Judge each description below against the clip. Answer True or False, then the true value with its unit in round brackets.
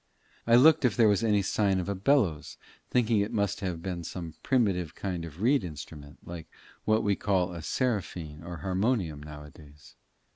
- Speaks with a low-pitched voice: True (95 Hz)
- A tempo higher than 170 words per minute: True (185 wpm)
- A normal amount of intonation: True (4.8 semitones)